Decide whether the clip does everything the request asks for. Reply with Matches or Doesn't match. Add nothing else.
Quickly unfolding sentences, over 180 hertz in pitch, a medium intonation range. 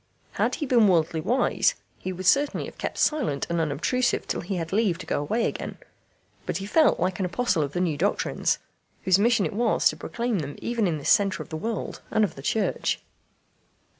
Doesn't match